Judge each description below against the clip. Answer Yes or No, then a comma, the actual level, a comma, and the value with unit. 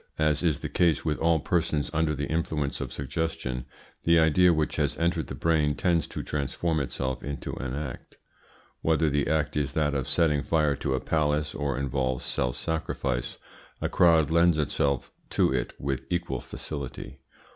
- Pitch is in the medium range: No, very low, 75 Hz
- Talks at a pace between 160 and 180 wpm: Yes, average, 170 wpm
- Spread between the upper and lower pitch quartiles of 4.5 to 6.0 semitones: No, average, 2.9 semitones